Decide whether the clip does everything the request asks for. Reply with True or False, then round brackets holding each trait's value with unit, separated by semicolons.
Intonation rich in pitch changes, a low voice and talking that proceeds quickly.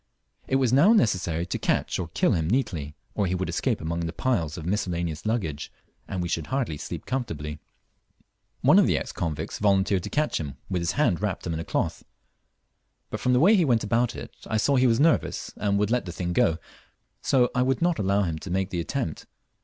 True (6.8 semitones; 95 Hz; 220 wpm)